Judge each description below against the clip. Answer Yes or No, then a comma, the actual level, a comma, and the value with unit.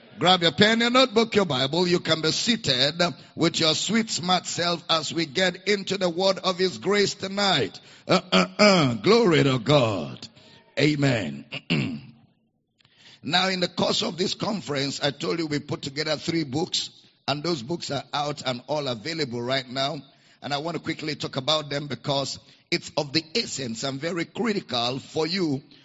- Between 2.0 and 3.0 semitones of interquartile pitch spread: No, average, 4.7 semitones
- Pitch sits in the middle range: Yes, medium, 160 Hz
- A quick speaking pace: No, average, 175 wpm